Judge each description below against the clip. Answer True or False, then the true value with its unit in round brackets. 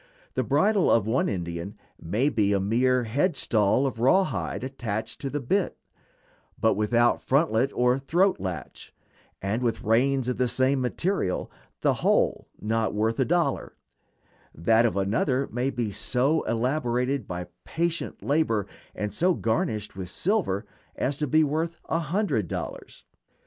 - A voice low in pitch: True (125 Hz)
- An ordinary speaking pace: True (150 wpm)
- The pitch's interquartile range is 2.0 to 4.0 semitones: False (4.8 semitones)